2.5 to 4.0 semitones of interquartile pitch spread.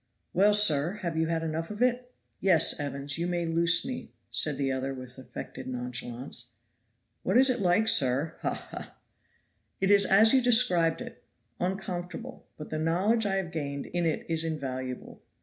No: wide, 5.6 semitones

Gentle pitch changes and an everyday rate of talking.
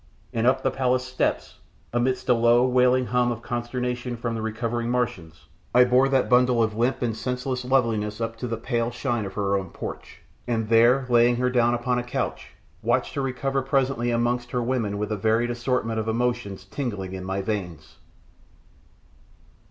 Yes: narrow, 2.0 semitones; average, 180 wpm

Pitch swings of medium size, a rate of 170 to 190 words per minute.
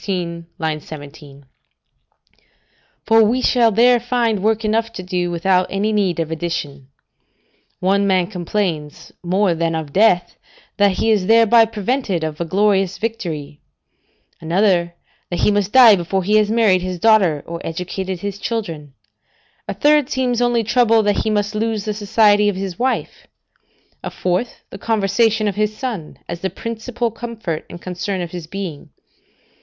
No: average, 4.3 semitones; average, 155 wpm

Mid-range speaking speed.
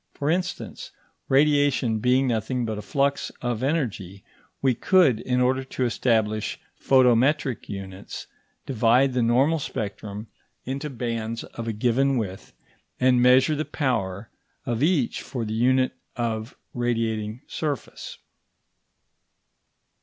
No: slow, 120 wpm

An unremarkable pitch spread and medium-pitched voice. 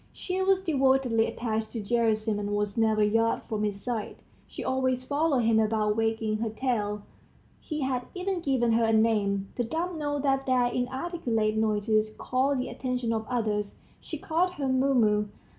No: average, 3.7 semitones; high, 235 Hz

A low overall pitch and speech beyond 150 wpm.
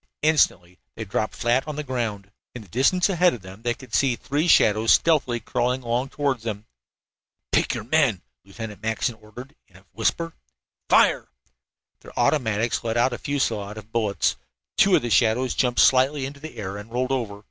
Yes: low, 120 Hz; average, 185 wpm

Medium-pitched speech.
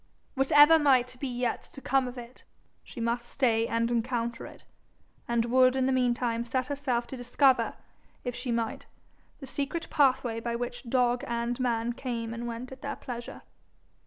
No: high, 245 Hz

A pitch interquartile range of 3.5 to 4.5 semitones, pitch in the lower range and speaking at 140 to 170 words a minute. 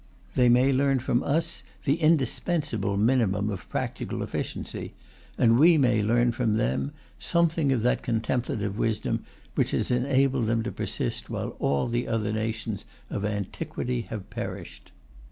Yes: average, 3.8 semitones; low, 120 Hz; average, 145 wpm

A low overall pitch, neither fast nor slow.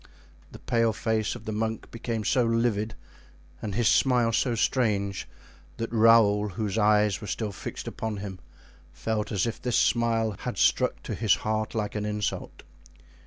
Yes: low, 110 Hz; average, 165 wpm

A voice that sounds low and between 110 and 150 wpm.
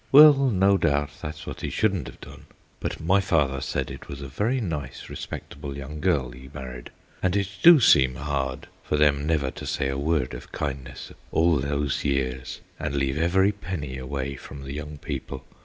No: very low, 75 Hz; average, 190 wpm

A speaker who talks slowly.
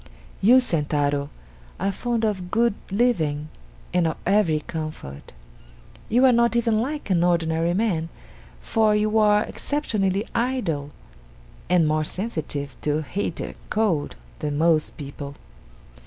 Yes: slow, 125 wpm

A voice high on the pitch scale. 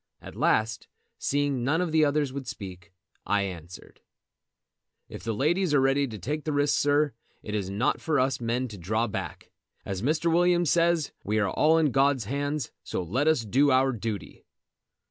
No: low, 135 Hz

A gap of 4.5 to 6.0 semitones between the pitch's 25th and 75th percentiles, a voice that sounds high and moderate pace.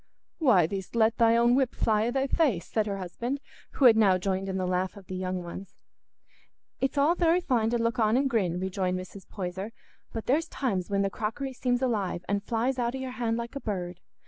No: average, 4.8 semitones; high, 220 Hz; fast, 225 wpm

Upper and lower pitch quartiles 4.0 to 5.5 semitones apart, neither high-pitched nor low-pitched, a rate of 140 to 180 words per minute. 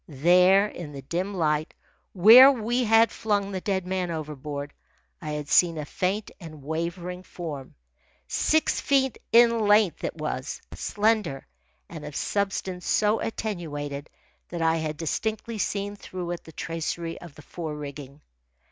Yes: average, 5.2 semitones; medium, 175 Hz; average, 145 wpm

